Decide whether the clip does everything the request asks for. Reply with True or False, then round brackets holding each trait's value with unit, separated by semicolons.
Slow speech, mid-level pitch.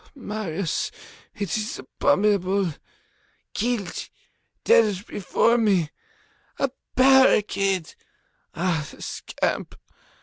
False (75 wpm; 205 Hz)